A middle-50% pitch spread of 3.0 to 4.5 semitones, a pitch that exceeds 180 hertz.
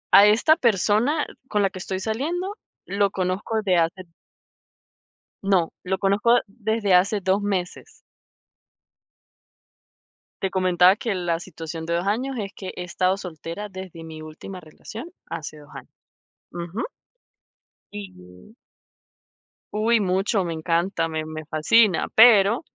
Yes: average, 3.6 semitones; high, 190 Hz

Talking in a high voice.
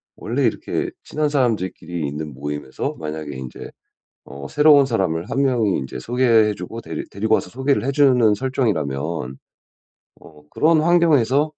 No: low, 110 Hz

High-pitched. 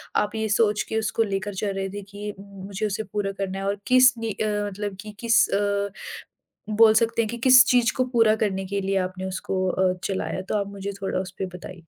Yes: high, 205 Hz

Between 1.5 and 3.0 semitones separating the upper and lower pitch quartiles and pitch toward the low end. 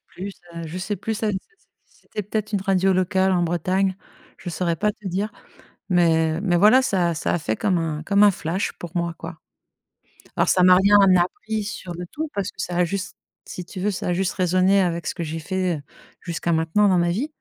No: narrow, 2.6 semitones; medium, 185 Hz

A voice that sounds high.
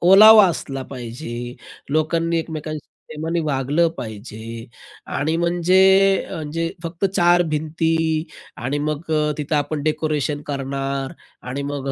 No: medium, 155 Hz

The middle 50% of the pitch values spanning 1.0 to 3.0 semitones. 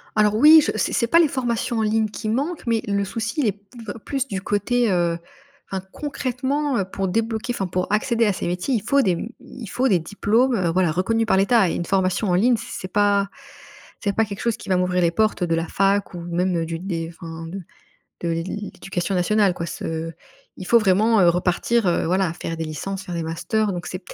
No: average, 4.2 semitones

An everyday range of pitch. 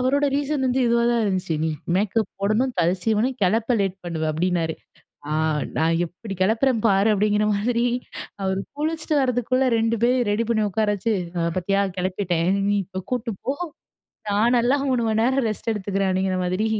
Yes: average, 4.4 semitones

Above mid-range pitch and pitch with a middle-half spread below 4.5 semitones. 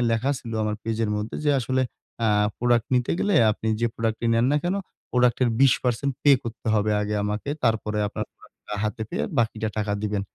No: low, 115 Hz; narrow, 2.5 semitones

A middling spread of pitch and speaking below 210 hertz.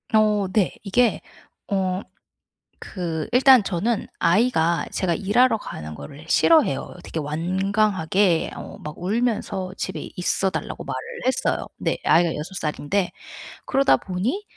Yes: average, 4.5 semitones; high, 190 Hz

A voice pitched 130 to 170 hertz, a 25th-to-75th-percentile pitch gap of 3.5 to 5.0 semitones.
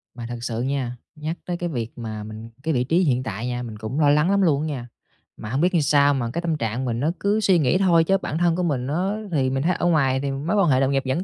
No: medium, 140 Hz; wide, 5.4 semitones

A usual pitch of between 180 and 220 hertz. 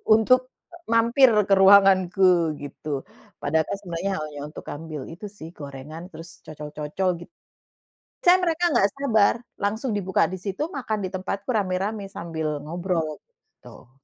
Yes: high, 190 Hz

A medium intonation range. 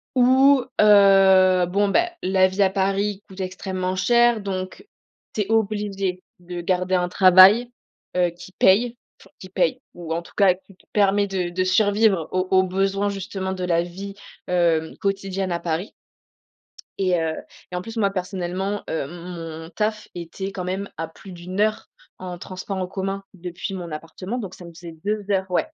No: narrow, 2.0 semitones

